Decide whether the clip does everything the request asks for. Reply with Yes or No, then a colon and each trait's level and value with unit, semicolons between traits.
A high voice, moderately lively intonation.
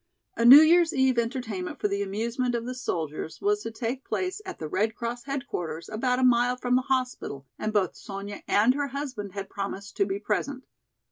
Yes: high, 235 Hz; average, 4.4 semitones